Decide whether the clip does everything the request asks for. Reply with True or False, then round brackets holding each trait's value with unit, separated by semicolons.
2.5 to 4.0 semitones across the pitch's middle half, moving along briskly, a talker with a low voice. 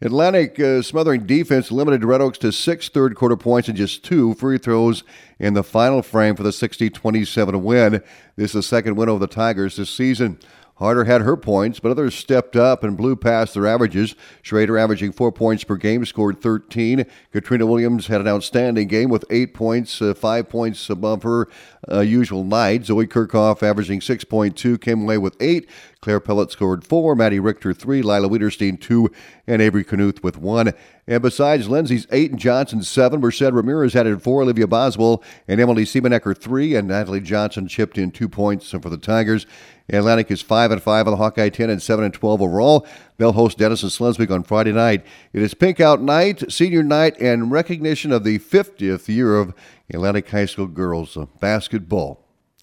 False (2.8 semitones; 185 wpm; 110 Hz)